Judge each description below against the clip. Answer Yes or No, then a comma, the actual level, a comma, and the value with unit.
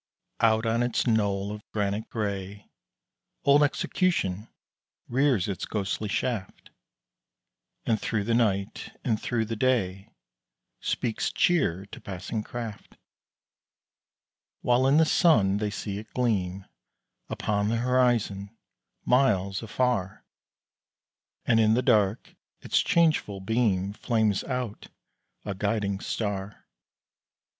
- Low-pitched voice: Yes, low, 110 Hz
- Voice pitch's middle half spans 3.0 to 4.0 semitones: Yes, average, 3.5 semitones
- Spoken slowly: Yes, slow, 110 wpm